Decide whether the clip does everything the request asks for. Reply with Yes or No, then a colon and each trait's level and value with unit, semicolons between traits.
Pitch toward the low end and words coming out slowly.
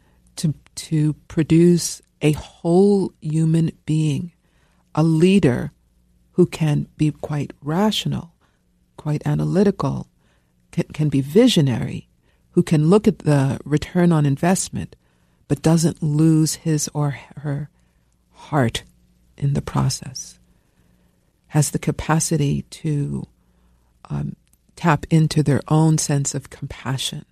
No: medium, 150 Hz; slow, 110 wpm